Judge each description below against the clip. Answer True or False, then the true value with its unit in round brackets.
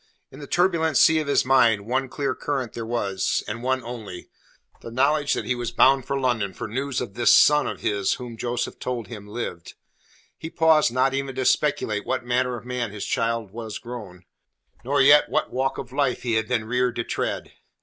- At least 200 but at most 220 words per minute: True (205 wpm)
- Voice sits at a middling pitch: False (125 Hz)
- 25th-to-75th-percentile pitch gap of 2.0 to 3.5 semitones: True (2.9 semitones)